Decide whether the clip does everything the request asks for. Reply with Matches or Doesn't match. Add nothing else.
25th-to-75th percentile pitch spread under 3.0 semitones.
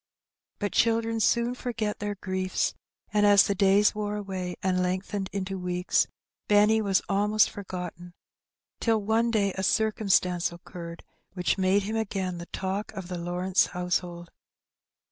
Matches